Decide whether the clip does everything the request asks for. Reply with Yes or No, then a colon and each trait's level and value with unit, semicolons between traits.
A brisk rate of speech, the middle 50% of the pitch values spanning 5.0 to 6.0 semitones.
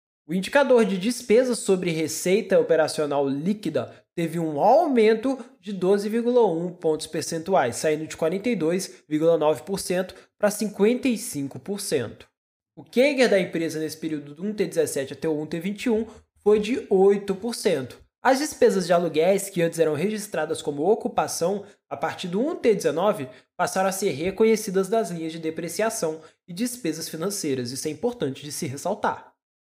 No: average, 130 wpm; wide, 5.4 semitones